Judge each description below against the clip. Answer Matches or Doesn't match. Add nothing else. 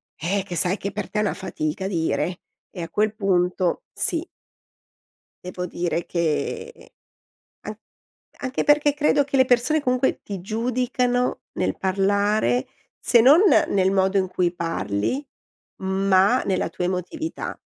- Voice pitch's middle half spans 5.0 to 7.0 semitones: Matches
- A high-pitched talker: Matches